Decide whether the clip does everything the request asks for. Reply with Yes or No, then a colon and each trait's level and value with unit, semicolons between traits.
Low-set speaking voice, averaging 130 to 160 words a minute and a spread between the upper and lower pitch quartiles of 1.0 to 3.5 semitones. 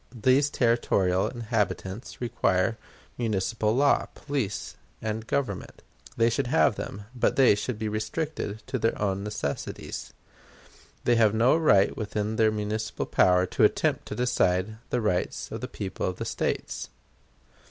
Yes: low, 110 Hz; average, 140 wpm; average, 3.1 semitones